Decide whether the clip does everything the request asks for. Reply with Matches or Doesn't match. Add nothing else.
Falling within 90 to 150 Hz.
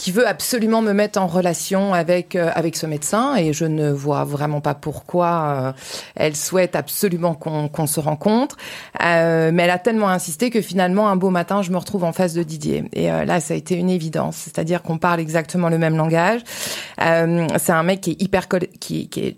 Doesn't match